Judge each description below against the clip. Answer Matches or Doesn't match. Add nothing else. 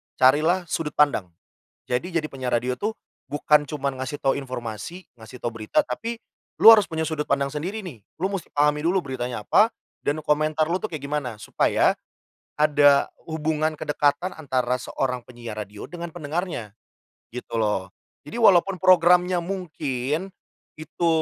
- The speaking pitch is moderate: Matches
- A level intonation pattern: Doesn't match